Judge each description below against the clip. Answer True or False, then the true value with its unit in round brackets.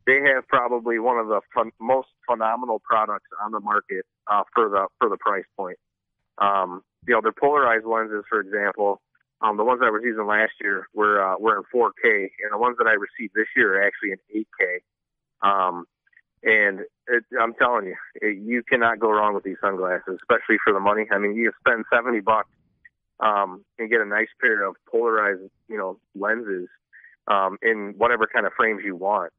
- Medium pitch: False (110 Hz)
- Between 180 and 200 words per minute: True (195 wpm)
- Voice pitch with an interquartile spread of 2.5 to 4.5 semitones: True (3.3 semitones)